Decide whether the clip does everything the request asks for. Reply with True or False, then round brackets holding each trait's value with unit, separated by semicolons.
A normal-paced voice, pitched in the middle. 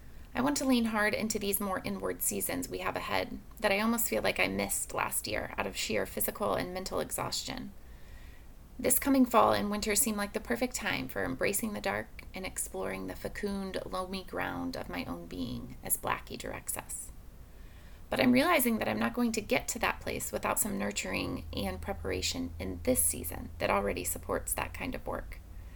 False (195 wpm; 100 Hz)